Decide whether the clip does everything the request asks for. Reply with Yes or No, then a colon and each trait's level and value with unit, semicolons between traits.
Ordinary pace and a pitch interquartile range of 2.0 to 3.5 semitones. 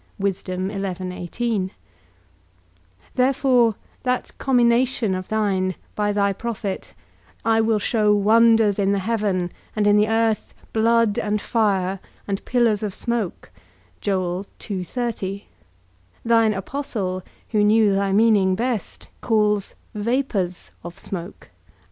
No: slow, 100 wpm; average, 2.9 semitones